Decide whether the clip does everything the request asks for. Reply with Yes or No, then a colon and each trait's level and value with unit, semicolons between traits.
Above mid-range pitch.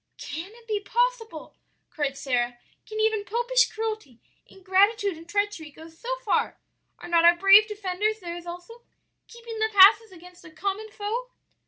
Yes: very high, 405 Hz